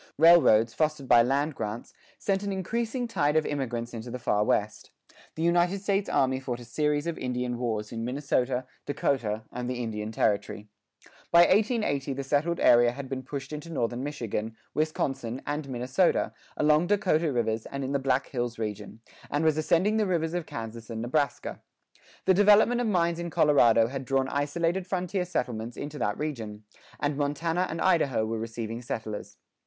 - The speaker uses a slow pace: No, average, 170 wpm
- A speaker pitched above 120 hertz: Yes, medium, 140 Hz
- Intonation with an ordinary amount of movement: No, wide, 5.9 semitones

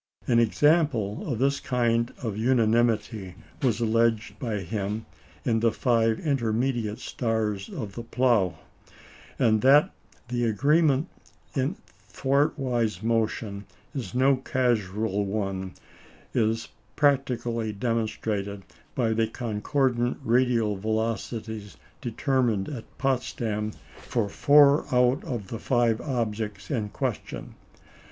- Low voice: Yes, low, 115 Hz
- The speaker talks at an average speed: No, slow, 105 wpm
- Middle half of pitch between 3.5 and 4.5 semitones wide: No, average, 3.0 semitones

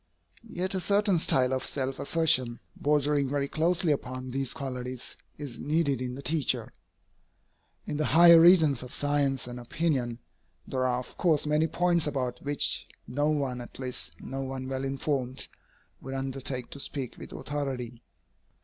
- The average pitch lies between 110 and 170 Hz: Yes, low, 135 Hz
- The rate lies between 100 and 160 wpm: Yes, average, 155 wpm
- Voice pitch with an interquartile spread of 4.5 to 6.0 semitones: No, average, 2.9 semitones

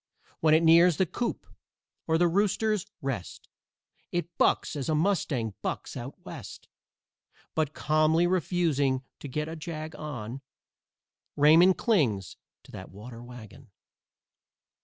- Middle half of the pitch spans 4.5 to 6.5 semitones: Yes, average, 4.8 semitones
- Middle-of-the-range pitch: Yes, medium, 155 Hz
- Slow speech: Yes, slow, 125 wpm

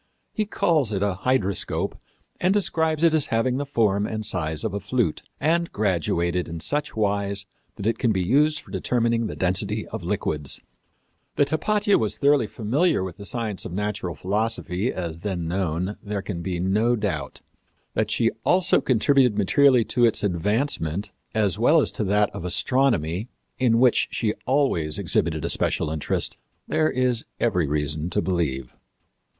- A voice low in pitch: Yes, low, 105 Hz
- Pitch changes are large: Yes, wide, 5.9 semitones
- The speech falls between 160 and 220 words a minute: Yes, average, 165 wpm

